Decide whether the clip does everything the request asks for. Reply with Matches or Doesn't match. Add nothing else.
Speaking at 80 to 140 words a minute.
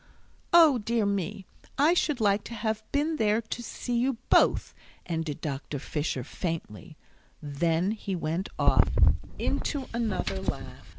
Matches